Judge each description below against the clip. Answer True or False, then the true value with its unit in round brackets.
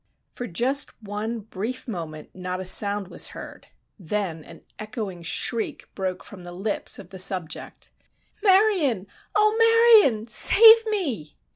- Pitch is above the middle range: True (215 Hz)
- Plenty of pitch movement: True (7.4 semitones)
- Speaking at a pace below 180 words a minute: True (135 wpm)